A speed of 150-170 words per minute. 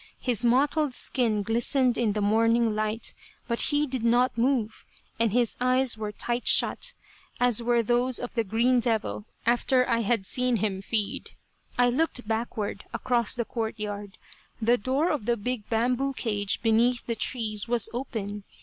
Yes: average, 165 wpm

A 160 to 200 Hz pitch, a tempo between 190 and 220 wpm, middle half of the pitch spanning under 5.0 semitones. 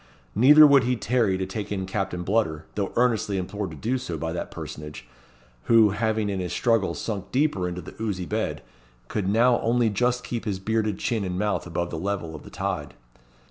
No: low, 105 Hz; average, 200 wpm; average, 4.0 semitones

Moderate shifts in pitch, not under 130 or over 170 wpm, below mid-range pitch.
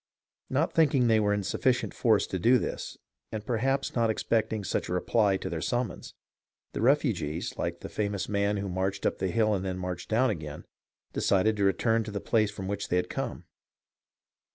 No: average, 3.3 semitones; average, 195 wpm; low, 105 Hz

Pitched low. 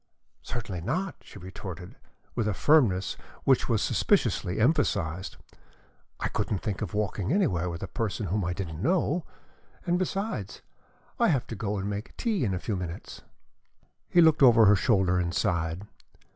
Yes: low, 100 Hz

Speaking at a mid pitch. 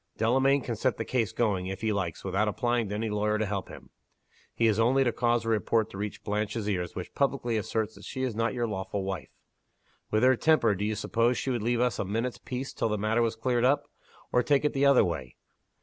No: low, 115 Hz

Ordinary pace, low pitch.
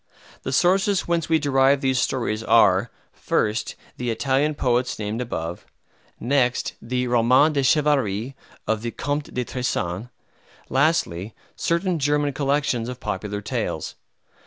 No: slow, 130 wpm; low, 130 Hz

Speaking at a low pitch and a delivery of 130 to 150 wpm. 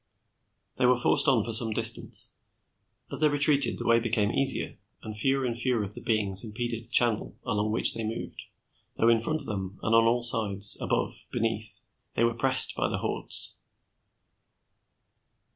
No: low, 115 Hz; average, 175 wpm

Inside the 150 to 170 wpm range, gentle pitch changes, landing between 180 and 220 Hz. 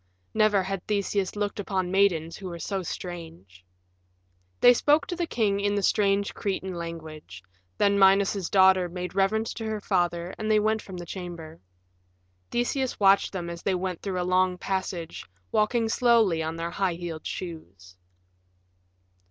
No: average, 160 wpm; average, 3.0 semitones; high, 190 Hz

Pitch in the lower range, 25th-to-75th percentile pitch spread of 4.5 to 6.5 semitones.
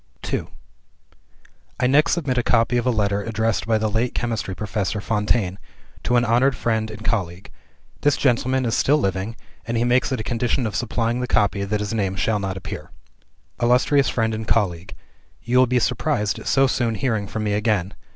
No: low, 115 Hz; average, 3.0 semitones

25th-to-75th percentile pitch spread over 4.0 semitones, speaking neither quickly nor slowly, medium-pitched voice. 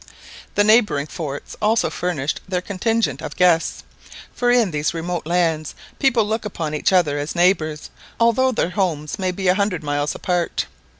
Yes: average, 5.1 semitones; average, 165 wpm; medium, 180 Hz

